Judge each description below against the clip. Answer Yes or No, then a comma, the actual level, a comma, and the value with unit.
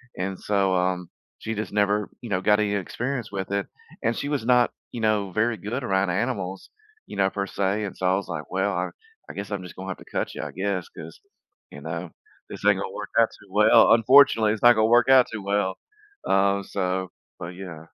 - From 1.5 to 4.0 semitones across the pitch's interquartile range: Yes, average, 2.8 semitones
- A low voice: Yes, low, 100 Hz